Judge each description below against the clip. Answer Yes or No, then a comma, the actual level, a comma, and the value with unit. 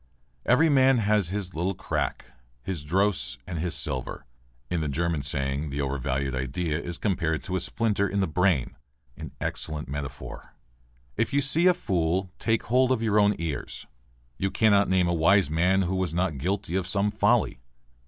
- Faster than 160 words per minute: Yes, average, 175 wpm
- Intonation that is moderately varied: Yes, average, 4.7 semitones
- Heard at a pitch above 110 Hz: No, very low, 90 Hz